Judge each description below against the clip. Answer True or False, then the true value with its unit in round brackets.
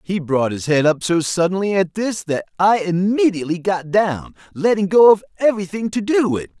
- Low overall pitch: False (185 Hz)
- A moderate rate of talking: True (190 wpm)